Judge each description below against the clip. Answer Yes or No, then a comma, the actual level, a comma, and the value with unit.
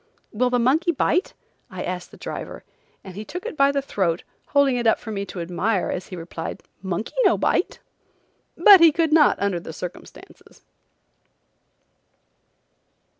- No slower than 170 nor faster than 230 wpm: No, average, 160 wpm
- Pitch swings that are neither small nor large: No, wide, 7.7 semitones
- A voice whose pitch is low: No, high, 220 Hz